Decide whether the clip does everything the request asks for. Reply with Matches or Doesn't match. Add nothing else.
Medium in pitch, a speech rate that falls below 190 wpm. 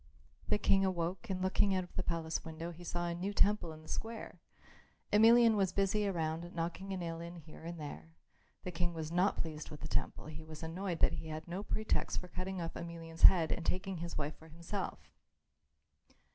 Doesn't match